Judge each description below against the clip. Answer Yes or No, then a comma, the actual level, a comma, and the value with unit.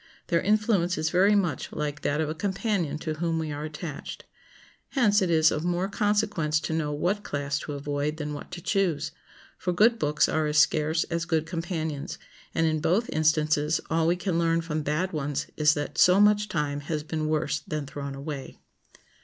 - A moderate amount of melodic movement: Yes, average, 3.0 semitones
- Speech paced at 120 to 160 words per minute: No, average, 195 wpm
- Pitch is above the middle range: No, medium, 160 Hz